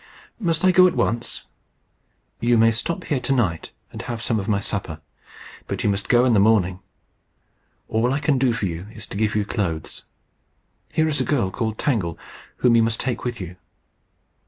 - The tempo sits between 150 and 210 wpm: Yes, average, 195 wpm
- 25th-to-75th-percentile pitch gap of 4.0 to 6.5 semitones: Yes, average, 4.3 semitones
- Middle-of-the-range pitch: No, low, 115 Hz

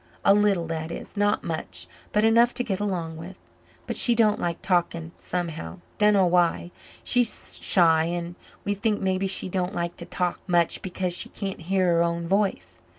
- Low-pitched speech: No, medium, 180 Hz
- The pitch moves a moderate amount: Yes, average, 3.1 semitones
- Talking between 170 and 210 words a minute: Yes, average, 180 wpm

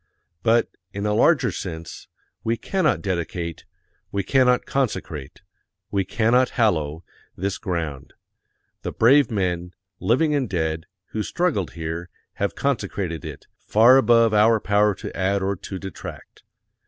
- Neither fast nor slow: No, slow, 130 wpm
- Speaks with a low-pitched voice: Yes, low, 100 Hz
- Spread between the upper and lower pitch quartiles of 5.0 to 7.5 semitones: Yes, average, 5.3 semitones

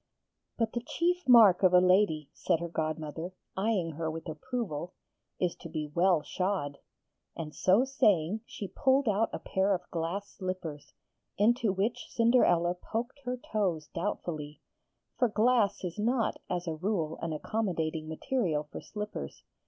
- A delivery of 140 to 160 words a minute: Yes, average, 150 wpm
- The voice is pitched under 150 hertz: No, medium, 185 Hz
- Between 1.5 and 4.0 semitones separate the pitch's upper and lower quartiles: No, average, 5.2 semitones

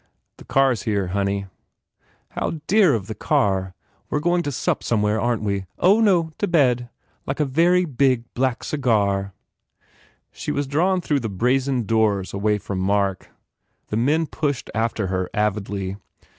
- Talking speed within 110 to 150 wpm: No, average, 170 wpm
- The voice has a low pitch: Yes, low, 115 Hz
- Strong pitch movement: Yes, wide, 6.3 semitones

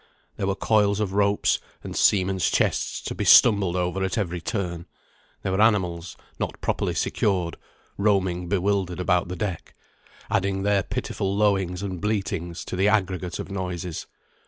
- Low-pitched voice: Yes, very low, 95 Hz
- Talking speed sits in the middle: Yes, average, 155 wpm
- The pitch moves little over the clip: Yes, narrow, 2.1 semitones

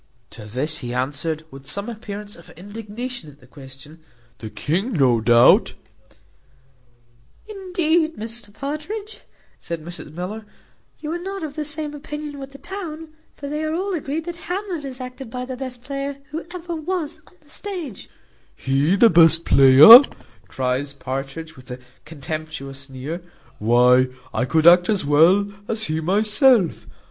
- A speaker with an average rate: Yes, average, 155 wpm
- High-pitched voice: Yes, high, 210 Hz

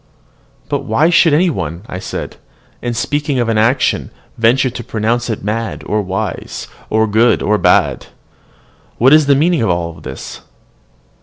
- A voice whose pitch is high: No, low, 115 Hz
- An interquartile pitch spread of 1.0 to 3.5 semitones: No, average, 4.3 semitones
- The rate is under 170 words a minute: Yes, average, 160 wpm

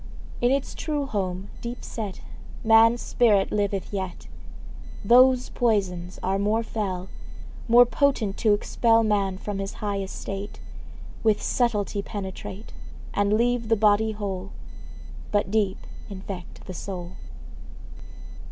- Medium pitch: No, high, 205 Hz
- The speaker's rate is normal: No, slow, 120 wpm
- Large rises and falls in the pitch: No, average, 2.7 semitones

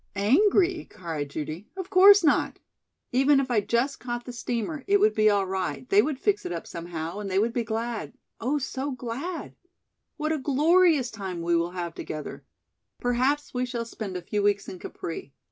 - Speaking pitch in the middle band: No, high, 235 Hz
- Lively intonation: Yes, wide, 7.5 semitones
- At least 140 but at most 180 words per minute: No, average, 190 wpm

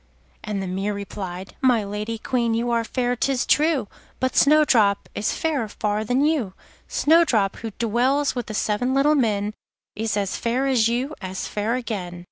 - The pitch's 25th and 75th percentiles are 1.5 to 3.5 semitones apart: No, average, 4.0 semitones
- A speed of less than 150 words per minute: No, average, 170 wpm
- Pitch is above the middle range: Yes, high, 230 Hz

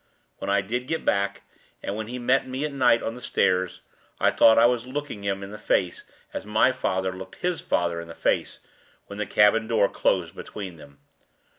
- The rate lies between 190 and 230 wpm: Yes, fast, 205 wpm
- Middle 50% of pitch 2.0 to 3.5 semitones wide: No, average, 4.6 semitones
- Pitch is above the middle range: No, low, 105 Hz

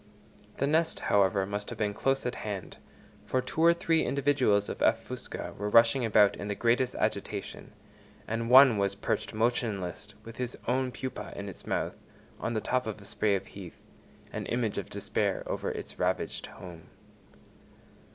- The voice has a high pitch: No, low, 110 Hz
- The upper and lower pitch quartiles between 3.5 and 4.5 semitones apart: Yes, average, 4.0 semitones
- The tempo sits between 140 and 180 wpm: Yes, average, 170 wpm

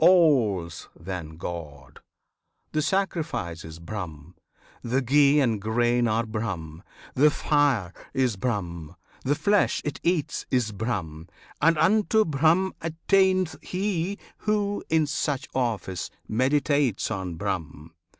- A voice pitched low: Yes, low, 125 Hz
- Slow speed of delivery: Yes, slow, 115 wpm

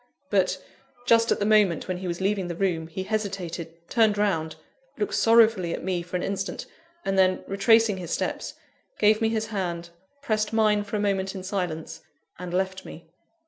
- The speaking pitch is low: No, high, 195 Hz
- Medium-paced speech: Yes, average, 185 wpm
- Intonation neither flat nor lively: Yes, average, 3.2 semitones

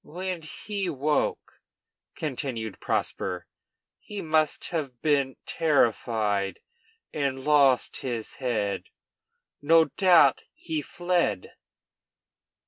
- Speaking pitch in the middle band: Yes, medium, 145 Hz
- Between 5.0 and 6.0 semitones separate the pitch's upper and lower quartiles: Yes, average, 5.3 semitones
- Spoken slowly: Yes, slow, 85 wpm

